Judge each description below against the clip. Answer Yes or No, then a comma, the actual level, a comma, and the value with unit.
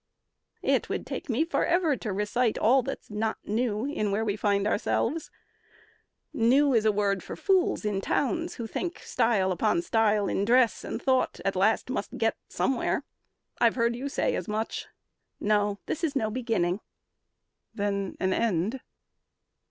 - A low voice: No, high, 225 Hz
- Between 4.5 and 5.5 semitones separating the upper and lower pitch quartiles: No, average, 4.0 semitones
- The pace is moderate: Yes, average, 160 wpm